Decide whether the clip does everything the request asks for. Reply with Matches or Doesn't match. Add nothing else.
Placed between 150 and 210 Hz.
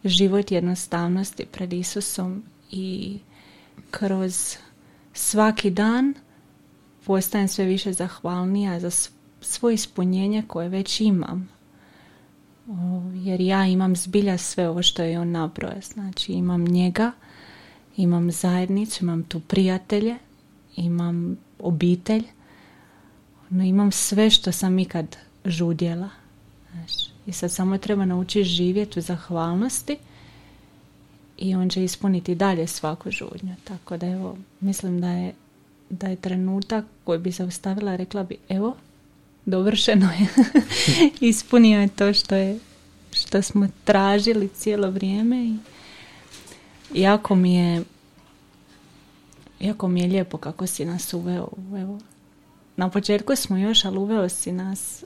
Matches